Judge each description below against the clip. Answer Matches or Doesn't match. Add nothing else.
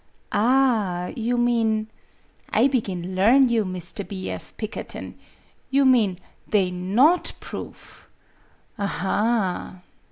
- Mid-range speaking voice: Doesn't match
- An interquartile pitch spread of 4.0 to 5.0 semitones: Matches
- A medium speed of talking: Doesn't match